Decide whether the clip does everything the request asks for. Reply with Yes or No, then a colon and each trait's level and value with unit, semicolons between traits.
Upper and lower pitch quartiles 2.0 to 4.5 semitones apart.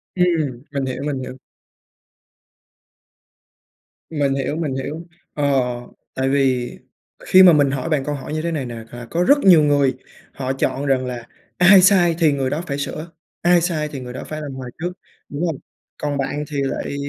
Yes: average, 3.6 semitones